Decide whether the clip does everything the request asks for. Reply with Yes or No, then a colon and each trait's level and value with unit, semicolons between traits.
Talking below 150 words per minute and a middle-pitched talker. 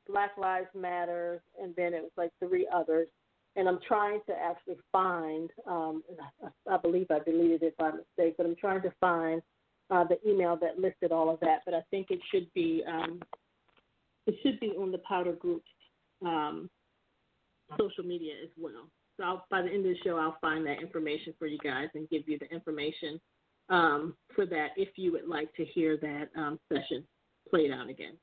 No: average, 195 wpm; medium, 170 Hz